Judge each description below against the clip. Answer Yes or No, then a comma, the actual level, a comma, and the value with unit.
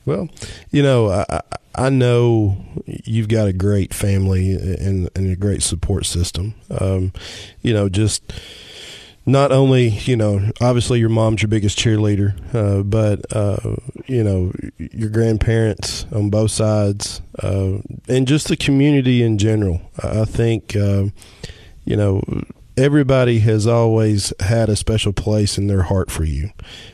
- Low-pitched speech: Yes, low, 105 Hz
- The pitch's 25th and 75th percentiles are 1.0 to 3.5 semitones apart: Yes, average, 2.8 semitones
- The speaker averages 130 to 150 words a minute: Yes, average, 145 wpm